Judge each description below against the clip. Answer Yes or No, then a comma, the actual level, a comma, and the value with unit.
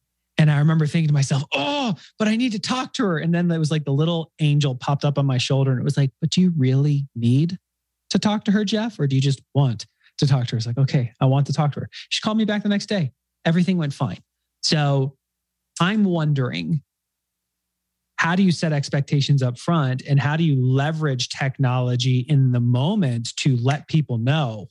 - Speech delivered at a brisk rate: Yes, fast, 225 wpm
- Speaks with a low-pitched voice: No, medium, 145 Hz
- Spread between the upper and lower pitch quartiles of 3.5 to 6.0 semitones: Yes, average, 4.3 semitones